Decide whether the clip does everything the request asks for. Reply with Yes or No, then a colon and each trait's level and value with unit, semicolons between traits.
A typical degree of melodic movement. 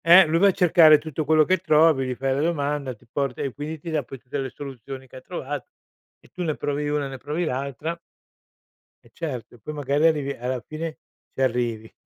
Yes: average, 3.1 semitones